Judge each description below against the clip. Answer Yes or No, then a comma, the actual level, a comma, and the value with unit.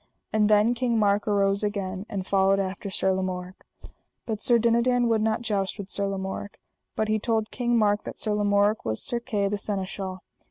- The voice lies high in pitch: Yes, high, 205 Hz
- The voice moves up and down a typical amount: No, narrow, 2.1 semitones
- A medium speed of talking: Yes, average, 190 wpm